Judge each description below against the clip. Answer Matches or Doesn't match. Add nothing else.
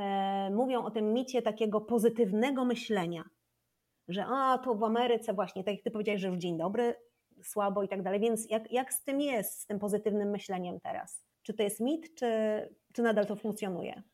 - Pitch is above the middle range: Matches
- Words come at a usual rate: Doesn't match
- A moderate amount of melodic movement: Matches